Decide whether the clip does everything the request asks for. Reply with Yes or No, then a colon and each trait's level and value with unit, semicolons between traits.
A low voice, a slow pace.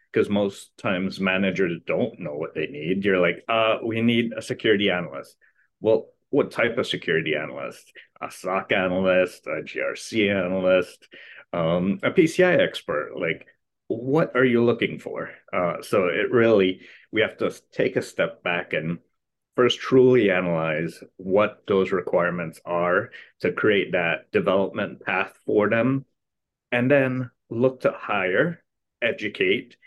No: low, 110 Hz; average, 145 wpm